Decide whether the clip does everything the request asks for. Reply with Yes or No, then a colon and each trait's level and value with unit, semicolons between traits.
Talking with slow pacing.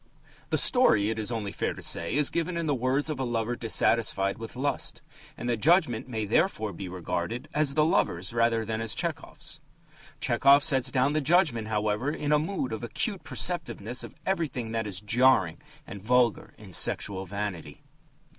No: average, 180 wpm